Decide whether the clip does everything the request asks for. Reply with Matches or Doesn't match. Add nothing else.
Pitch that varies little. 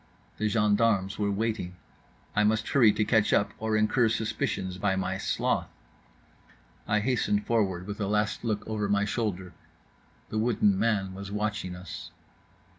Matches